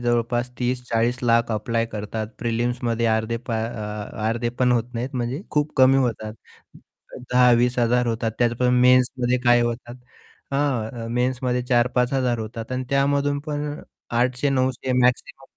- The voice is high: No, low, 120 Hz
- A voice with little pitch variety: Yes, narrow, 1.5 semitones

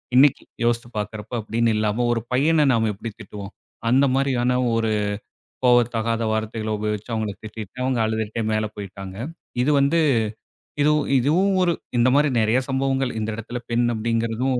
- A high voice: No, low, 115 Hz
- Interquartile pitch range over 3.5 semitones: No, average, 3.1 semitones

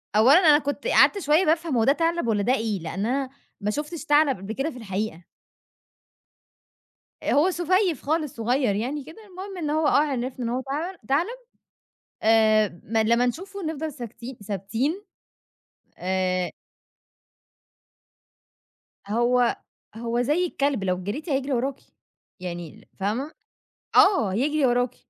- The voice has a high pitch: Yes, very high, 260 Hz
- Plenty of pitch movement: Yes, wide, 6.0 semitones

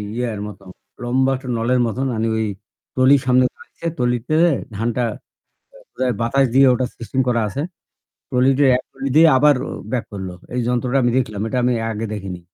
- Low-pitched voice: Yes, low, 125 Hz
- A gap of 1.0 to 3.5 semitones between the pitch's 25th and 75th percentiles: Yes, narrow, 2.5 semitones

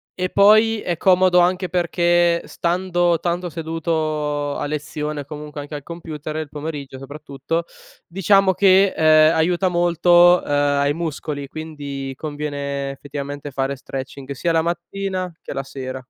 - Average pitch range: Yes, average, 3.4 semitones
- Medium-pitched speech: Yes, medium, 155 Hz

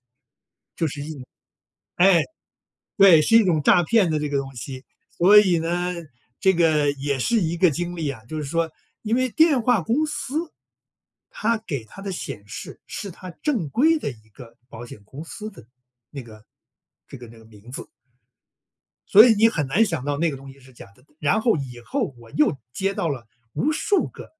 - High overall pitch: No, medium, 165 Hz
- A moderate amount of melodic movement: No, wide, 7.5 semitones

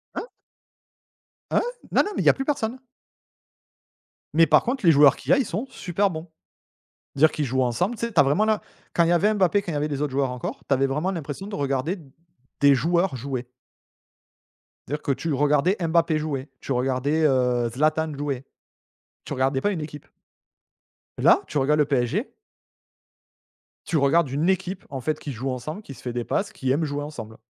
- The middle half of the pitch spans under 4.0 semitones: No, average, 4.5 semitones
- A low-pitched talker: No, medium, 150 Hz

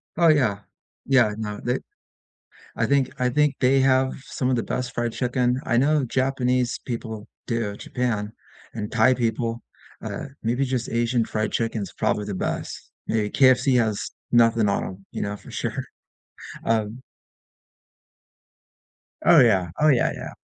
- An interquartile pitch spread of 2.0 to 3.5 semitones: Yes, average, 2.8 semitones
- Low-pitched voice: Yes, low, 120 Hz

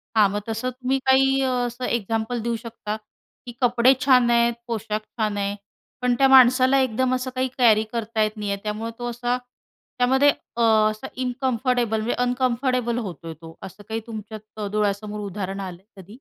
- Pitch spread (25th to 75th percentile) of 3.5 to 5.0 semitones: No, average, 2.9 semitones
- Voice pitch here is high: Yes, high, 230 Hz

